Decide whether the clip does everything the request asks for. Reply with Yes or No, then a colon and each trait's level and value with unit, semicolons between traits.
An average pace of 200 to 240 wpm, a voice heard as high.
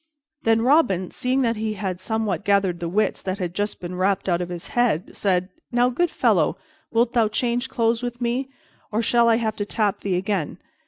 Yes: fast, 205 wpm; high, 215 Hz